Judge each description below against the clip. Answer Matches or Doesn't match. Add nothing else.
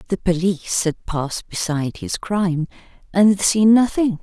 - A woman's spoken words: Matches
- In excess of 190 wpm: Doesn't match